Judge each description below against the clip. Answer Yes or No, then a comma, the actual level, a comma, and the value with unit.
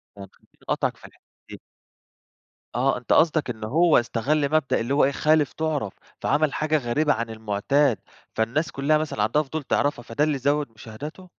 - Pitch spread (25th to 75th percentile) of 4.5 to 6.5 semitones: Yes, average, 4.8 semitones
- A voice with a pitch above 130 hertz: Yes, medium, 140 Hz